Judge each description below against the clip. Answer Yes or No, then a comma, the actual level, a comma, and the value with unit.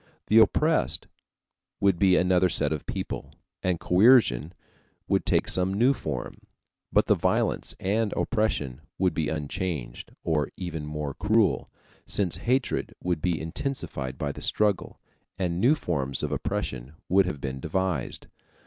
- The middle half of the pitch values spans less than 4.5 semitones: No, average, 5.2 semitones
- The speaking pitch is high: No, very low, 90 Hz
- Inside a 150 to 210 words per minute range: No, average, 140 wpm